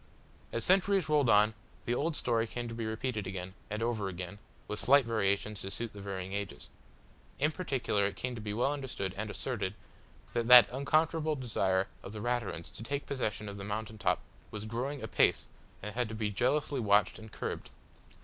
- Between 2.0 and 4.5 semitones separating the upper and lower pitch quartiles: Yes, average, 4.1 semitones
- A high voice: No, low, 110 Hz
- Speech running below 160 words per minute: No, average, 190 wpm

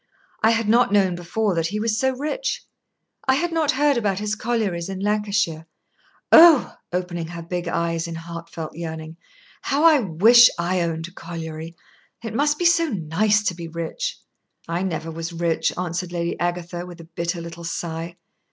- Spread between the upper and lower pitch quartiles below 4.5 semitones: No, average, 4.8 semitones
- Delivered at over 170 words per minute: Yes, average, 180 wpm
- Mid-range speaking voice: Yes, medium, 175 Hz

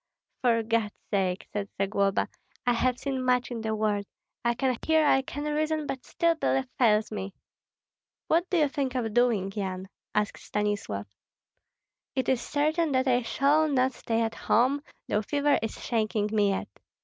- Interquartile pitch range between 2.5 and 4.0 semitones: No, average, 4.8 semitones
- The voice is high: Yes, high, 240 Hz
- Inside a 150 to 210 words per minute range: Yes, average, 170 wpm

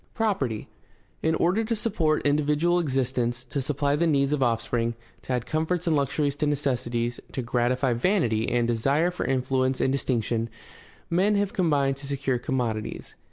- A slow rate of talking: No, average, 160 wpm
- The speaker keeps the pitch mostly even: No, average, 4.5 semitones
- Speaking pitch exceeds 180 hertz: No, medium, 140 Hz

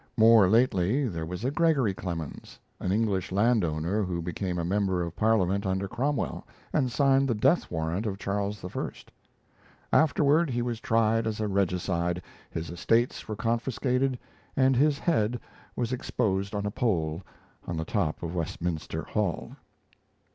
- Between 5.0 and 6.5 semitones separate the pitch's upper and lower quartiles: Yes, average, 5.3 semitones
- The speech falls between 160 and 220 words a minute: No, average, 150 wpm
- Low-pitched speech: Yes, low, 105 Hz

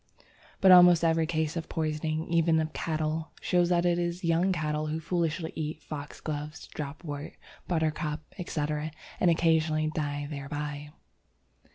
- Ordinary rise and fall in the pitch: No, narrow, 1.8 semitones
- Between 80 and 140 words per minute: Yes, slow, 135 wpm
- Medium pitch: Yes, medium, 160 Hz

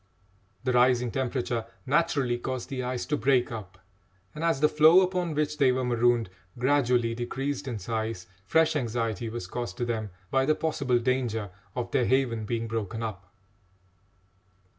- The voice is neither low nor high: No, low, 125 Hz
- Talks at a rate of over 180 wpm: No, average, 160 wpm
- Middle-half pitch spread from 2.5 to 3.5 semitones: Yes, average, 3.1 semitones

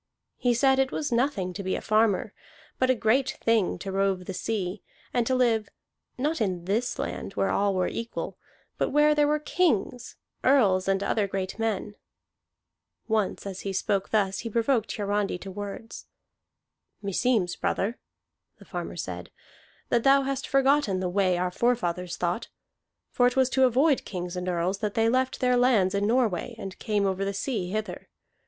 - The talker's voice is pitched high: Yes, high, 215 Hz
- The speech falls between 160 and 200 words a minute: Yes, average, 175 wpm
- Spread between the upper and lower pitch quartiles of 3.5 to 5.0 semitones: Yes, average, 4.6 semitones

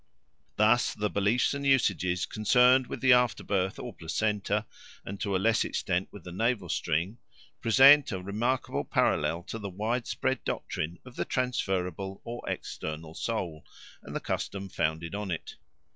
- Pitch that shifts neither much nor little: Yes, average, 4.9 semitones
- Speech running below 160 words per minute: Yes, average, 150 wpm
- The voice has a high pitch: No, low, 100 Hz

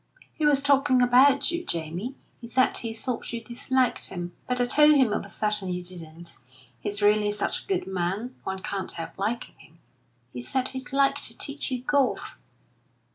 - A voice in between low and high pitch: No, high, 235 Hz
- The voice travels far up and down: Yes, wide, 5.7 semitones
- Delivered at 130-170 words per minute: No, average, 185 wpm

